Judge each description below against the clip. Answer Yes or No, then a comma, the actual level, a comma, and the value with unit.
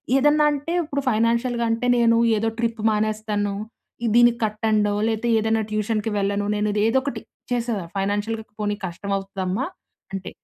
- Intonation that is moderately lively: No, narrow, 2.2 semitones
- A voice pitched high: Yes, high, 220 Hz